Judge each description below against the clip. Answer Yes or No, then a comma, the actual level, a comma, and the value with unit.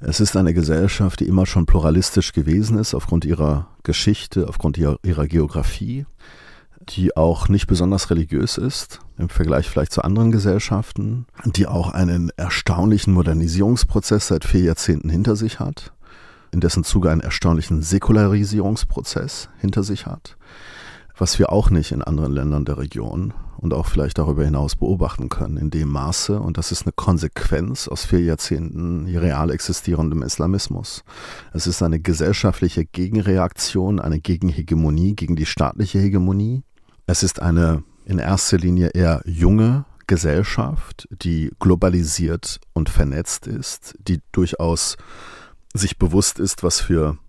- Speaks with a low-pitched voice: Yes, very low, 90 Hz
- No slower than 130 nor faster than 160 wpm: Yes, average, 140 wpm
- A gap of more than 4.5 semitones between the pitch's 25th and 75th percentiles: No, average, 3.4 semitones